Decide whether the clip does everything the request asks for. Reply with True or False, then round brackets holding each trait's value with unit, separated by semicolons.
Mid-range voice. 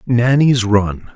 False (115 Hz)